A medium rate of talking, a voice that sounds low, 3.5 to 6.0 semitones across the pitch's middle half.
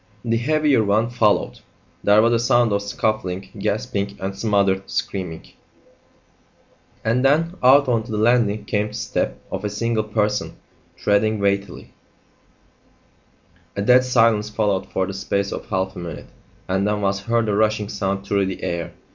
No: average, 160 wpm; low, 105 Hz; average, 2.7 semitones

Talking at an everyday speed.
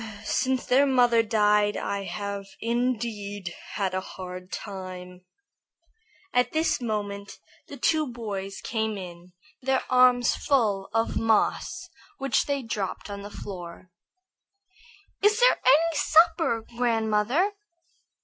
No: slow, 115 wpm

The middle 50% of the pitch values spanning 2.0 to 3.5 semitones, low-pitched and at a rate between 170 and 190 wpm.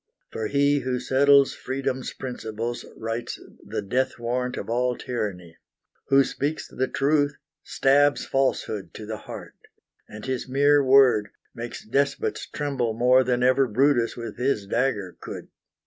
No: average, 2.9 semitones; low, 125 Hz; average, 140 wpm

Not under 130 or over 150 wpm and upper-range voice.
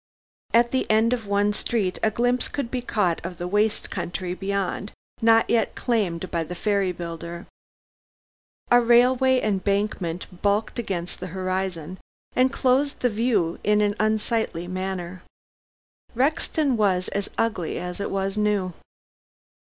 Yes: average, 140 wpm; high, 205 Hz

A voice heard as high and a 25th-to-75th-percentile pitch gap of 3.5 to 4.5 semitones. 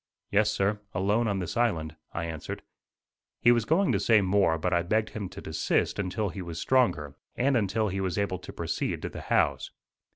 No: low, 100 Hz; average, 3.8 semitones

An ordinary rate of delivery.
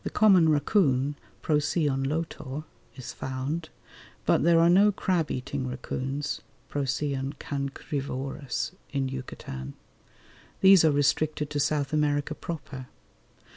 No: slow, 110 wpm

